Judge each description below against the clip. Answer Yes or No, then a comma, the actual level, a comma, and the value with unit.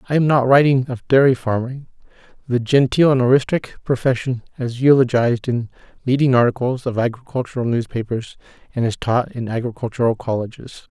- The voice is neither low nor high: No, low, 125 Hz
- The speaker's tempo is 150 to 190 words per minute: No, average, 140 wpm